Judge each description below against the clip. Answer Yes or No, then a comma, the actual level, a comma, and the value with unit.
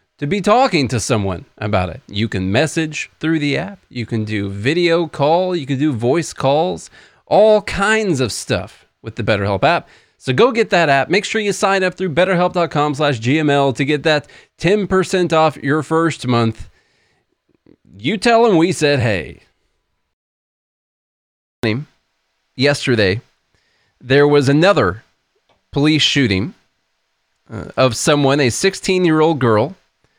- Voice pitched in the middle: Yes, medium, 145 Hz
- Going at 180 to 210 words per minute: No, slow, 135 wpm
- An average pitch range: No, wide, 7.4 semitones